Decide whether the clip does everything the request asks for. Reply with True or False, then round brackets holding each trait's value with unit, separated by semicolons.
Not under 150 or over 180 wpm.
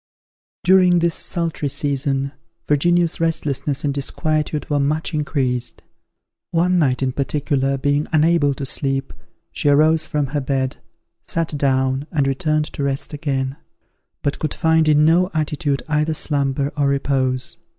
False (140 wpm)